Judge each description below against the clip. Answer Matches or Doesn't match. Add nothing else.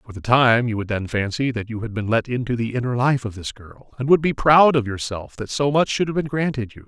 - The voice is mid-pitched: Doesn't match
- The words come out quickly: Matches